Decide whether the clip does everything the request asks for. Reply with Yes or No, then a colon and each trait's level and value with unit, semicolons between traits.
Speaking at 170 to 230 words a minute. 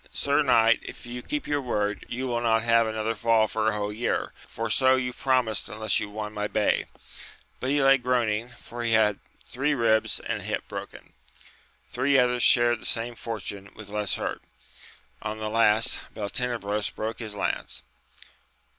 Yes: average, 175 wpm